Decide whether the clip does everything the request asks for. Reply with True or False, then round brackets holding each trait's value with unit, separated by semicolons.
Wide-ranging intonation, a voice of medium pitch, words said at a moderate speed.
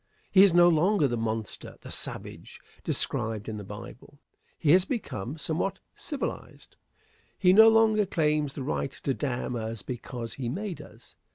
True (8.1 semitones; 150 Hz; 160 wpm)